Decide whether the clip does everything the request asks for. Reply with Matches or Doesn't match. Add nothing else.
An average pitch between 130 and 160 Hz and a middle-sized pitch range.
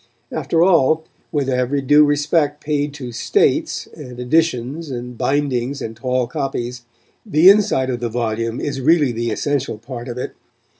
Matches